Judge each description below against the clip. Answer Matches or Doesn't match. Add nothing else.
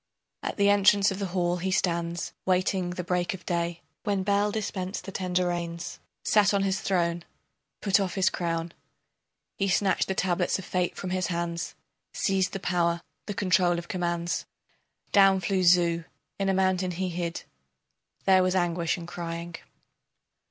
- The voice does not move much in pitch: Matches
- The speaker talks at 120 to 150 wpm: Doesn't match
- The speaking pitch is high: Doesn't match